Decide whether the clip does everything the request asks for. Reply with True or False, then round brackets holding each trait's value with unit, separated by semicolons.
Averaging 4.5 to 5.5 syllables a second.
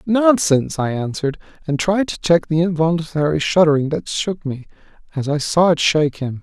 True (5.4 syllables/s)